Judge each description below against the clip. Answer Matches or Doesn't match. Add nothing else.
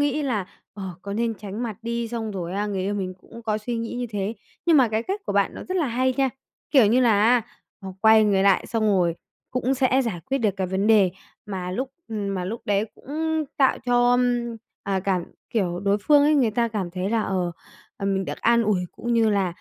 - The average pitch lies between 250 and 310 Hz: Doesn't match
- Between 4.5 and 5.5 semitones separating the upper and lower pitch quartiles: Doesn't match